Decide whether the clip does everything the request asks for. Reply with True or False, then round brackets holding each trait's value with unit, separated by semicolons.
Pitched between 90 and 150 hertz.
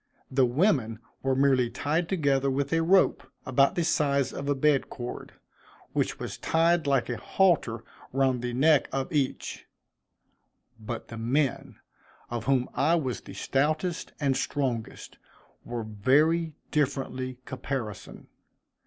True (135 Hz)